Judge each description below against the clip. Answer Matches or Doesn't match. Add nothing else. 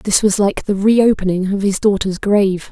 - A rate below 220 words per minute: Matches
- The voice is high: Matches